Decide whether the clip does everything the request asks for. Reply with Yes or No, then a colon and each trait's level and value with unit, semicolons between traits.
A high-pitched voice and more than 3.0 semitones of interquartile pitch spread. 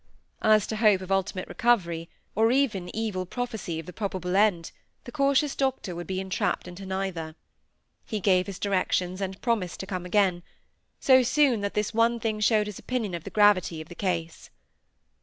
Yes: high, 195 Hz; average, 3.6 semitones